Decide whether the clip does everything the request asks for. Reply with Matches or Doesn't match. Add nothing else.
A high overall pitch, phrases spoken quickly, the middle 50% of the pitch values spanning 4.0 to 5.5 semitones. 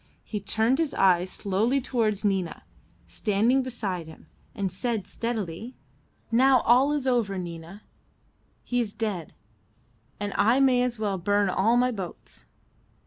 Doesn't match